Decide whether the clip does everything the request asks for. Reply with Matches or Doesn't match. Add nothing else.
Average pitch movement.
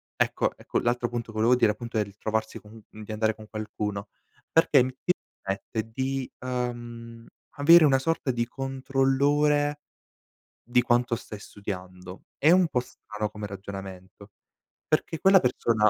Matches